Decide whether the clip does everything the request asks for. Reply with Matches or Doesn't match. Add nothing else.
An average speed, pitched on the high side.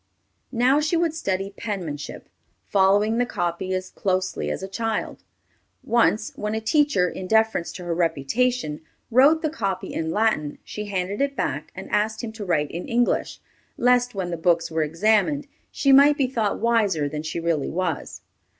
Matches